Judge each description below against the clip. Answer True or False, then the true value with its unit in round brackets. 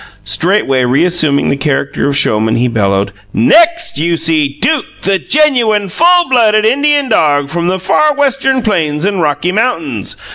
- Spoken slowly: False (150 wpm)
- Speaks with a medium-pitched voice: True (175 Hz)